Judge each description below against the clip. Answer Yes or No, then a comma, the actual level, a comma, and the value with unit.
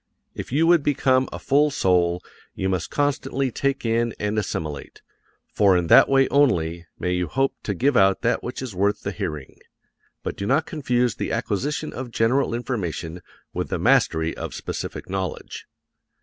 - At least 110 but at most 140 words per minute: No, average, 170 wpm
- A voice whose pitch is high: No, low, 115 Hz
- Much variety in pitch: Yes, wide, 7.0 semitones